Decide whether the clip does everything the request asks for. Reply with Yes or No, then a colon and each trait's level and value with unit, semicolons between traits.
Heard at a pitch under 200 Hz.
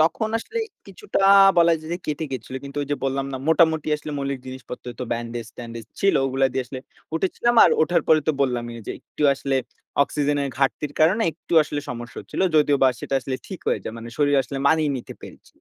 Yes: medium, 140 Hz